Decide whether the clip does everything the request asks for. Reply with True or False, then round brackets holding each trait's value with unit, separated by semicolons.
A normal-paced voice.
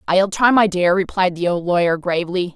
False (210 wpm)